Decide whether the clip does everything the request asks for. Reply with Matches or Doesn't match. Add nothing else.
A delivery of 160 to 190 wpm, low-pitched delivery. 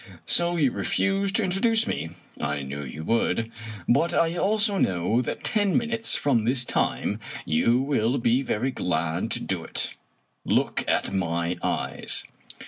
Doesn't match